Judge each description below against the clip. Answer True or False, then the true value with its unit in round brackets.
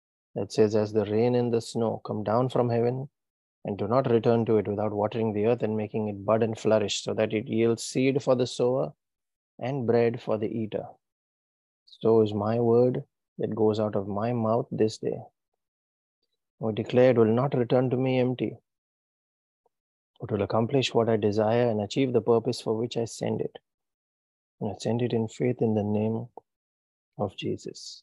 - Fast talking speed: False (185 wpm)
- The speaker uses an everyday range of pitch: False (2.2 semitones)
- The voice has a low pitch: True (110 Hz)